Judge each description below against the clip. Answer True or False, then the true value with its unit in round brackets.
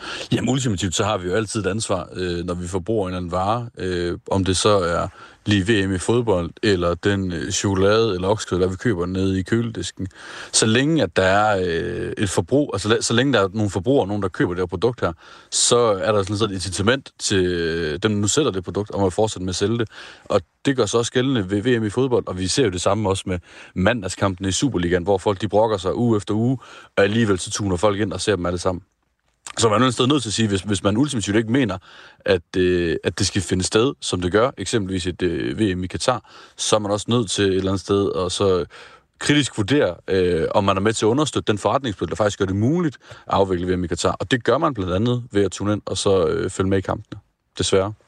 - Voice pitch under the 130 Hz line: True (100 Hz)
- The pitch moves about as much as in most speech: True (3.1 semitones)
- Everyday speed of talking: False (255 wpm)